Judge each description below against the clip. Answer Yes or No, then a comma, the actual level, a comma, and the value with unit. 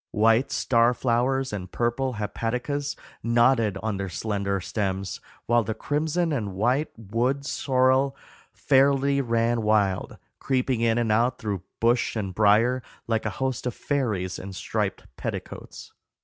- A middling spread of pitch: Yes, average, 3.8 semitones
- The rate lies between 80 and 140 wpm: Yes, slow, 135 wpm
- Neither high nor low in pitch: No, low, 115 Hz